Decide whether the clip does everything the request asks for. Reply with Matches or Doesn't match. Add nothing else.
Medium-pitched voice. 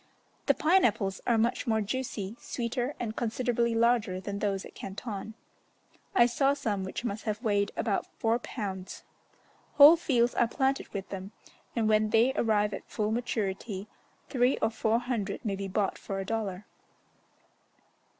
Doesn't match